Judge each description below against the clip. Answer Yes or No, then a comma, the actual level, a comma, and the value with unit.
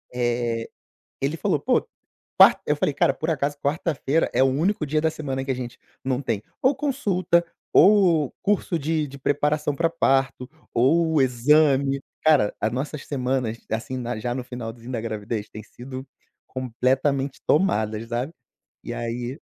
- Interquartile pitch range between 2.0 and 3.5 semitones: No, average, 4.0 semitones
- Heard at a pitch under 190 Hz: Yes, low, 135 Hz